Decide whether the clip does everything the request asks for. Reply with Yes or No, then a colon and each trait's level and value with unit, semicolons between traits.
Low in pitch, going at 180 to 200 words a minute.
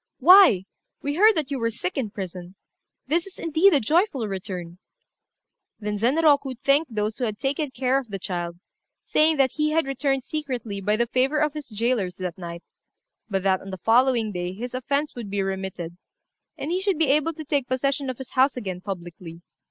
No: very high, 250 Hz; average, 195 wpm